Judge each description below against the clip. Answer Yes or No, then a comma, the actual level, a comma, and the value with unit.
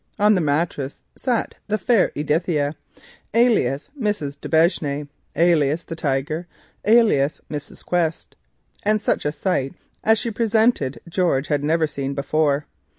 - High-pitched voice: No, medium, 160 Hz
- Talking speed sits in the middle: No, slow, 130 wpm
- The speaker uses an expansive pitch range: Yes, wide, 6.3 semitones